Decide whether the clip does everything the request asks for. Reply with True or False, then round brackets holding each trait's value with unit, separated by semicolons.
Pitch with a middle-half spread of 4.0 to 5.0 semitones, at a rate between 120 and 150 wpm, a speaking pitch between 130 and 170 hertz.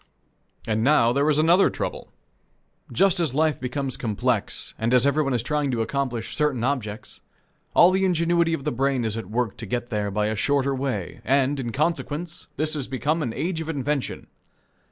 False (4.5 semitones; 185 wpm; 135 Hz)